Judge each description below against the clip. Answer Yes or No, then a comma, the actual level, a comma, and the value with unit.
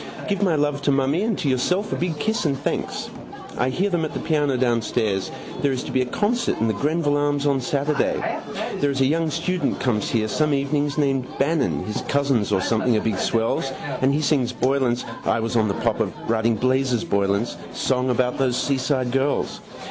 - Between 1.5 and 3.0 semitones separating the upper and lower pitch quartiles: No, average, 3.4 semitones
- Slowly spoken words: No, fast, 205 wpm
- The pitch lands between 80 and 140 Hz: Yes, low, 135 Hz